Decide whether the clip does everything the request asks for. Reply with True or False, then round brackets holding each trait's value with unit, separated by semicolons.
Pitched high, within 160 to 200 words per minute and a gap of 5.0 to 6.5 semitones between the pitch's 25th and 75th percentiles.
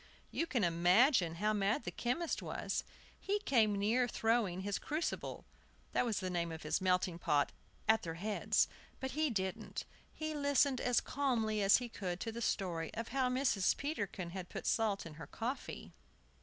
True (215 Hz; 175 wpm; 5.6 semitones)